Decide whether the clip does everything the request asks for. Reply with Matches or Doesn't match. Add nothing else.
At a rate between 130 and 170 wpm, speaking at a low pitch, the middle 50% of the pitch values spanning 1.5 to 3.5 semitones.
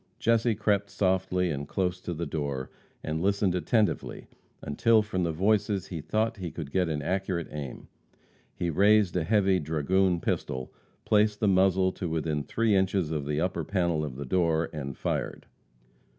Doesn't match